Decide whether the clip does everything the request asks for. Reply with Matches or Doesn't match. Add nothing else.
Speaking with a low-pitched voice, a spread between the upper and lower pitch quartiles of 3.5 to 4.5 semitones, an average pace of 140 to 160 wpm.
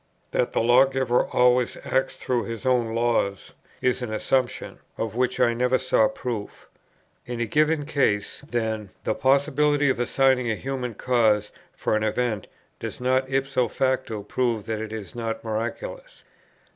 Doesn't match